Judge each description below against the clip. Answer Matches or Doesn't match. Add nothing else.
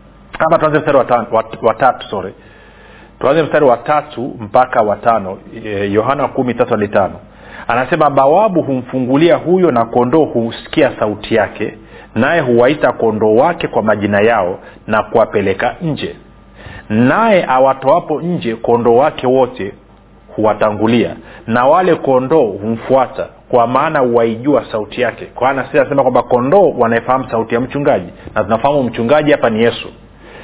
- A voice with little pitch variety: Doesn't match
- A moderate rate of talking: Matches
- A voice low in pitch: Matches